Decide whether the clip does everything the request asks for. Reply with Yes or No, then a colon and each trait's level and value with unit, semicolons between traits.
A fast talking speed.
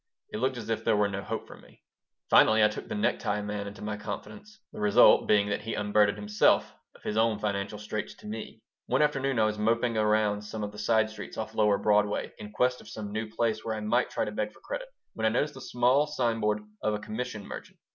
Yes: fast, 240 wpm